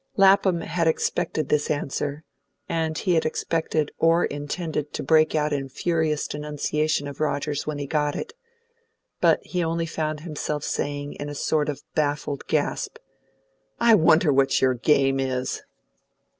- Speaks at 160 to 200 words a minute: No, average, 150 wpm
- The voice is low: No, medium, 150 Hz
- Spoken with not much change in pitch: Yes, narrow, 2.0 semitones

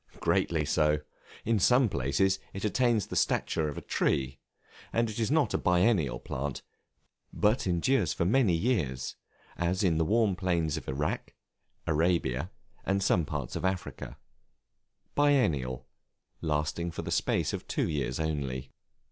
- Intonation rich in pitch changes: Yes, wide, 6.0 semitones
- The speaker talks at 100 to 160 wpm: Yes, average, 140 wpm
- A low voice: Yes, very low, 85 Hz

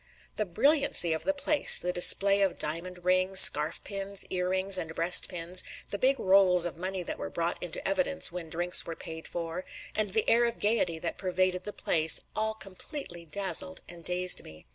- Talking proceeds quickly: No, average, 190 wpm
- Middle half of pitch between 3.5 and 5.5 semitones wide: No, average, 2.8 semitones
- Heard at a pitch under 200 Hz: Yes, medium, 185 Hz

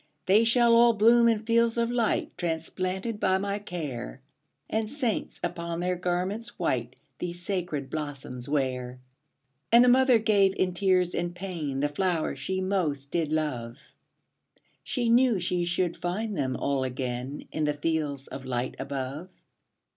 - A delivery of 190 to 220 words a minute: No, average, 150 wpm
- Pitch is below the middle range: No, medium, 175 Hz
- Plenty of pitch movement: Yes, wide, 6.7 semitones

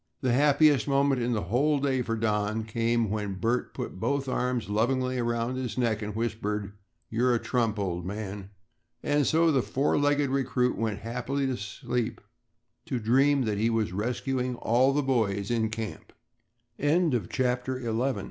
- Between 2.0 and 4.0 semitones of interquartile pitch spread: Yes, average, 3.5 semitones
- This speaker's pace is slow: No, average, 165 wpm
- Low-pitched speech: Yes, low, 120 Hz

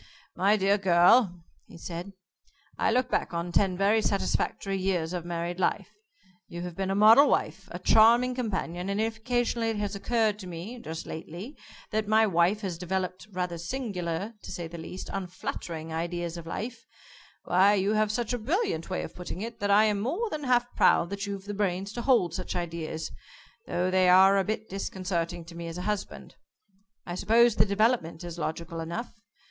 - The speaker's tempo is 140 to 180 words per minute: No, average, 190 wpm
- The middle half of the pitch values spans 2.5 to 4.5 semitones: Yes, average, 4.0 semitones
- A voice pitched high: Yes, high, 195 Hz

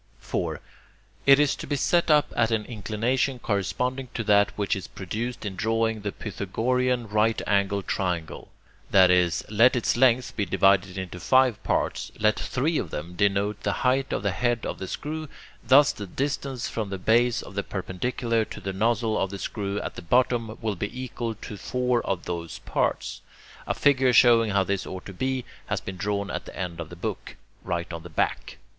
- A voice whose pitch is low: Yes, low, 110 Hz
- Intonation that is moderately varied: Yes, average, 4.3 semitones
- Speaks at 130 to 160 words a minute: No, average, 195 wpm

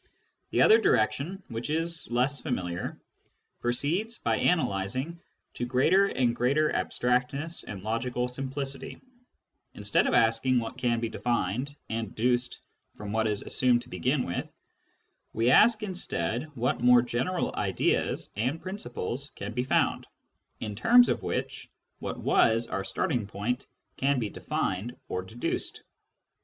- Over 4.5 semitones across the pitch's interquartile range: No, average, 4.0 semitones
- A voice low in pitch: Yes, low, 125 Hz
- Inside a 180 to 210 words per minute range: No, slow, 135 wpm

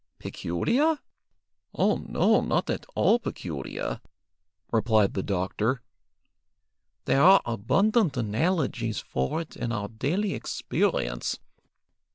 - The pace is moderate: No, slow, 100 wpm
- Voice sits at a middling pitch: No, low, 120 Hz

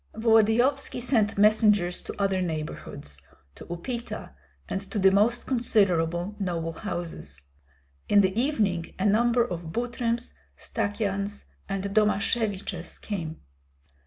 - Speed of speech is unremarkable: No, slow, 110 wpm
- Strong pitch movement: No, average, 4.2 semitones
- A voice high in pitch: Yes, high, 205 Hz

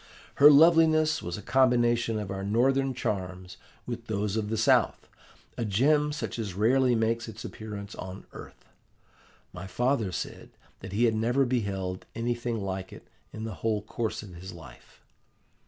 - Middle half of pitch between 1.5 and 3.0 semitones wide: No, average, 3.9 semitones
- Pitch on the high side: No, low, 110 Hz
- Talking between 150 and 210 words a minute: Yes, average, 160 wpm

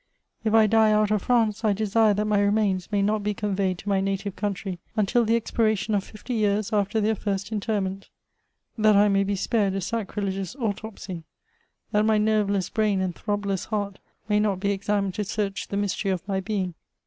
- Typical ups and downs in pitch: No, narrow, 1.6 semitones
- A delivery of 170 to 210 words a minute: Yes, average, 195 wpm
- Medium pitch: No, high, 205 Hz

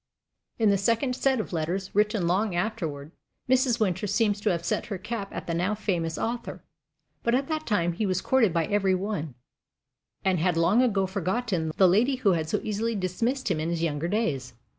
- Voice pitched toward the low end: No, high, 195 Hz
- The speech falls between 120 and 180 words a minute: No, average, 200 wpm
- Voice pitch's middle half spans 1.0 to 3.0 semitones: No, average, 4.8 semitones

